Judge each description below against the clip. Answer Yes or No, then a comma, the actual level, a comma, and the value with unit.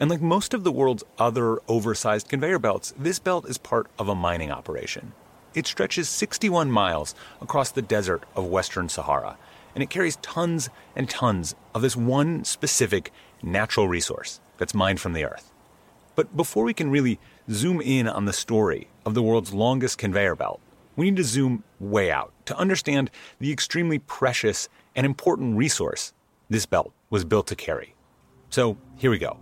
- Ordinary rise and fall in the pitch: No, wide, 5.9 semitones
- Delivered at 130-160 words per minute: No, average, 175 wpm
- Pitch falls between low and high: No, low, 125 Hz